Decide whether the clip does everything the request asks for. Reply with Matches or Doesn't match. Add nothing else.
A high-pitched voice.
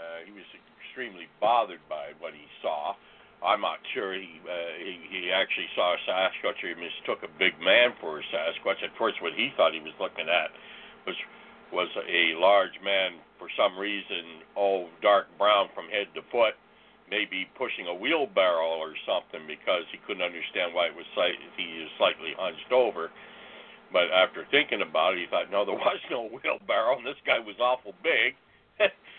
Doesn't match